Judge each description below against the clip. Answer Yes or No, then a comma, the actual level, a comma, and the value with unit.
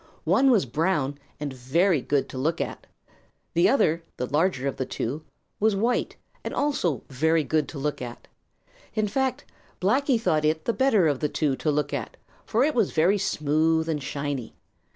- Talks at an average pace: Yes, average, 180 wpm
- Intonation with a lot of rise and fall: Yes, wide, 5.8 semitones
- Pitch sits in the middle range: Yes, medium, 160 Hz